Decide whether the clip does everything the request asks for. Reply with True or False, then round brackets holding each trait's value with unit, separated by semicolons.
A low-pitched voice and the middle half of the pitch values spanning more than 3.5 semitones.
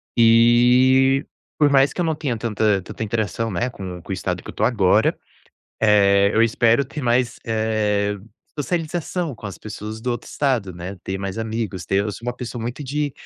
True (115 Hz; 3.9 semitones)